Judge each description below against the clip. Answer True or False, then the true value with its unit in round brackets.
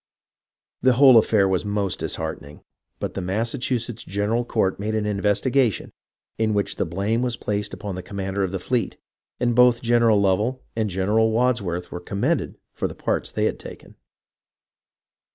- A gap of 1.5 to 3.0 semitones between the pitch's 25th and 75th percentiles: False (3.5 semitones)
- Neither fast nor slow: True (170 wpm)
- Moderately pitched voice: False (105 Hz)